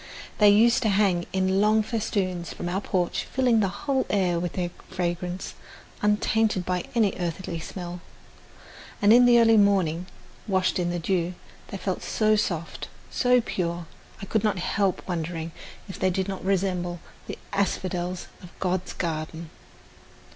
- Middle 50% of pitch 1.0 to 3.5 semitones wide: Yes, average, 3.0 semitones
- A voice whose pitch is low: No, medium, 185 Hz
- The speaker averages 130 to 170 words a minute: Yes, average, 155 wpm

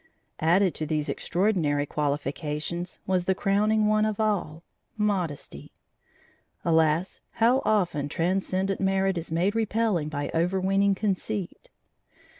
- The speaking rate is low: Yes, slow, 110 wpm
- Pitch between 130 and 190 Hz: Yes, medium, 185 Hz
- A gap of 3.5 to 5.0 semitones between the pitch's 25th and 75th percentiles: Yes, average, 4.1 semitones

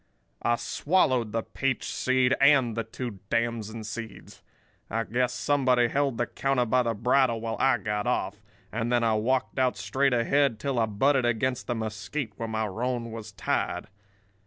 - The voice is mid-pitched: No, low, 120 Hz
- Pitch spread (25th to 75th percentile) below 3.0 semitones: Yes, narrow, 2.6 semitones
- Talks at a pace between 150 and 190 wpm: Yes, average, 170 wpm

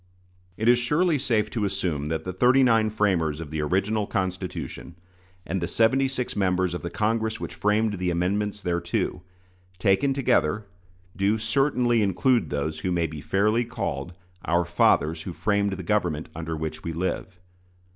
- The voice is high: No, very low, 95 Hz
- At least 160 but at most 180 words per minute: Yes, average, 165 wpm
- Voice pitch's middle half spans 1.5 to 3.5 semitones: No, average, 4.5 semitones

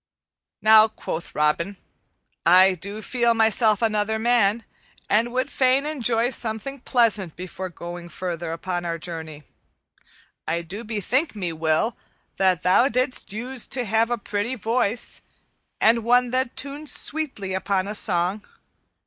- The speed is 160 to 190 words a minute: No, slow, 135 wpm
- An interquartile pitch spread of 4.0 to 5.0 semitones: Yes, average, 4.7 semitones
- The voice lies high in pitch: Yes, high, 215 Hz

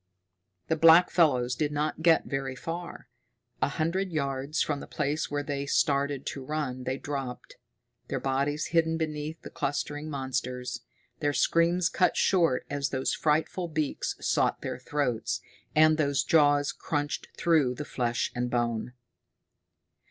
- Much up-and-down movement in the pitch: No, average, 3.0 semitones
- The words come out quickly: No, slow, 135 wpm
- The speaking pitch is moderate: Yes, medium, 145 Hz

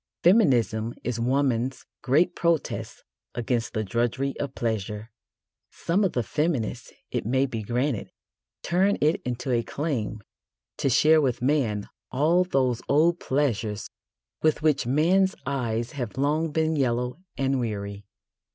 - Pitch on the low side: Yes, low, 130 Hz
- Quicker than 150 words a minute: No, slow, 135 wpm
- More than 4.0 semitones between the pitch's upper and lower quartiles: Yes, average, 4.7 semitones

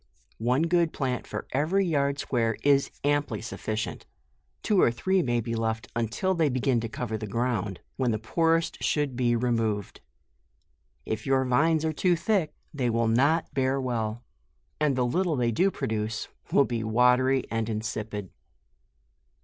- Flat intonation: No, average, 4.6 semitones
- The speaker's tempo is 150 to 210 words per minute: Yes, average, 155 wpm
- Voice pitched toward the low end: Yes, low, 125 Hz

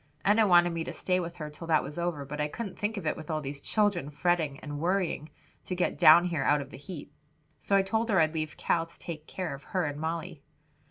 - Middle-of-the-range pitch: Yes, medium, 165 Hz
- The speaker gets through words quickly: Yes, fast, 255 wpm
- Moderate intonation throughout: Yes, average, 3.4 semitones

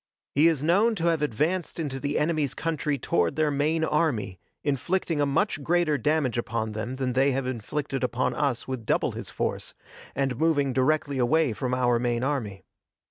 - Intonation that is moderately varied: Yes, average, 3.8 semitones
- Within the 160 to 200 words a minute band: Yes, average, 180 wpm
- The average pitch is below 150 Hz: Yes, medium, 140 Hz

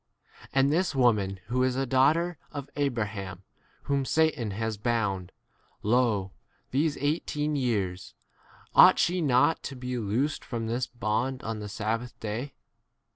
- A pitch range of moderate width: Yes, average, 4.6 semitones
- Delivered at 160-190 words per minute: No, slow, 135 wpm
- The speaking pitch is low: Yes, low, 125 Hz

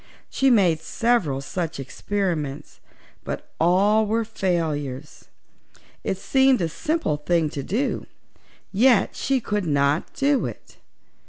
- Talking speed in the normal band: No, slow, 115 wpm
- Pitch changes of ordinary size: No, wide, 7.2 semitones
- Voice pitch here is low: No, medium, 185 Hz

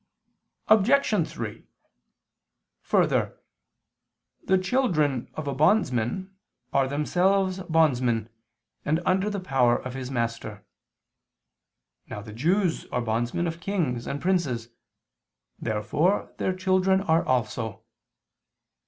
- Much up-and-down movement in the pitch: Yes, wide, 7.4 semitones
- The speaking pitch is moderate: Yes, medium, 155 Hz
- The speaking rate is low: Yes, slow, 100 wpm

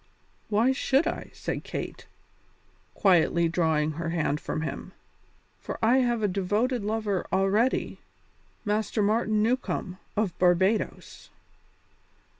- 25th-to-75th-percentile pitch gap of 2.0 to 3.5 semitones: No, average, 4.2 semitones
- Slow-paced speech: Yes, slow, 110 wpm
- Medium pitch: No, high, 205 Hz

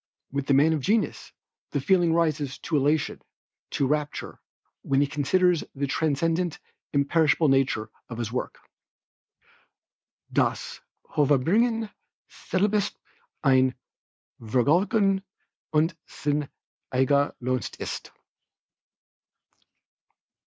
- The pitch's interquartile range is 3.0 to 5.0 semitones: Yes, average, 4.0 semitones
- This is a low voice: No, medium, 150 Hz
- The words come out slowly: Yes, slow, 95 wpm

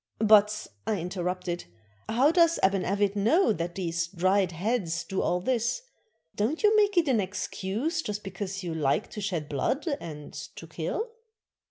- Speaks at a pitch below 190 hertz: No, high, 200 Hz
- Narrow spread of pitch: No, average, 5.1 semitones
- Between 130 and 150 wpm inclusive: No, average, 160 wpm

